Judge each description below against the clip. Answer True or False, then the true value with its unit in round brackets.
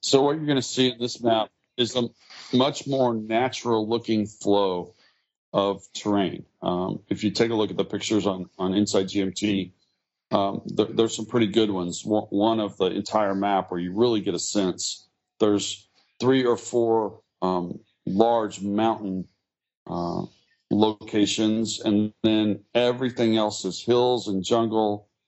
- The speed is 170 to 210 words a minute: False (155 wpm)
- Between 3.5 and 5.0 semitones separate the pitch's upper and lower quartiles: False (2.8 semitones)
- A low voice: True (105 Hz)